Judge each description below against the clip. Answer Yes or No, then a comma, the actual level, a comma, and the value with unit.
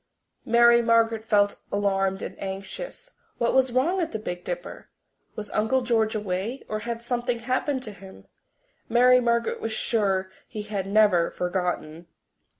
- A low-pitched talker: No, high, 220 Hz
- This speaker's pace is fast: No, average, 150 wpm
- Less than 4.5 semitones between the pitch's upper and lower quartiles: Yes, average, 3.5 semitones